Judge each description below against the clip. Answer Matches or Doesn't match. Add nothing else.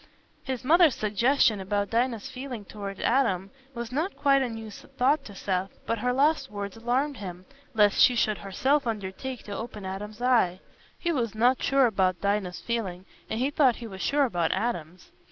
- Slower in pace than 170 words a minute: Doesn't match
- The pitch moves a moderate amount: Matches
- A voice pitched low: Doesn't match